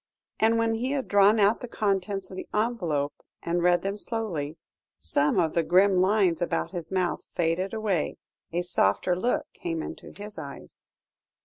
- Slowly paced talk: No, average, 170 wpm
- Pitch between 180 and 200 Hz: Yes, high, 190 Hz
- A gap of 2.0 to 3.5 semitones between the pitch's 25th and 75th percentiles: No, average, 3.9 semitones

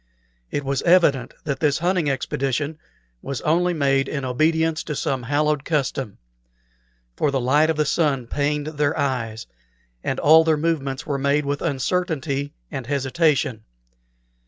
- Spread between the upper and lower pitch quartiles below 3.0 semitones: Yes, narrow, 2.5 semitones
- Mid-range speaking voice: Yes, medium, 145 Hz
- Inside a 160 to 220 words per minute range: No, average, 145 wpm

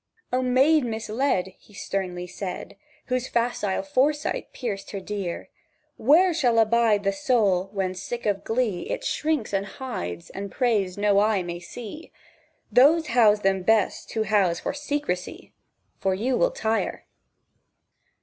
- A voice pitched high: Yes, high, 220 Hz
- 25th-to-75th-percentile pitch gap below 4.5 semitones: No, average, 4.8 semitones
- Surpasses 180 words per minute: No, average, 140 wpm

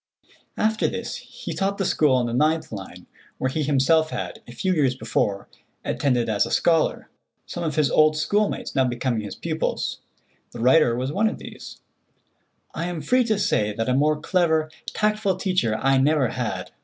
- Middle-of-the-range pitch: Yes, medium, 155 Hz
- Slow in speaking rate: No, average, 185 wpm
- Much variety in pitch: Yes, wide, 6.1 semitones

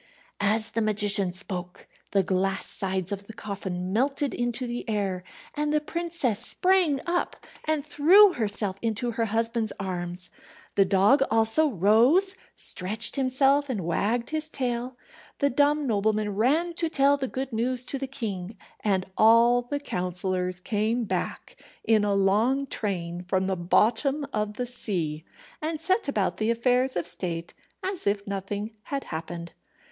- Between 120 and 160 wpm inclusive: Yes, average, 150 wpm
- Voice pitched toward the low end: No, high, 225 Hz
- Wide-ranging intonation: Yes, wide, 5.8 semitones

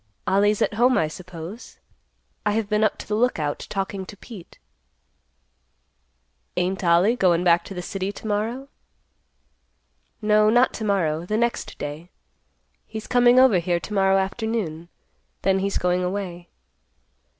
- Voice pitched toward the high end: Yes, high, 195 Hz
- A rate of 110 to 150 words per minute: Yes, average, 145 wpm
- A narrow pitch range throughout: No, average, 3.4 semitones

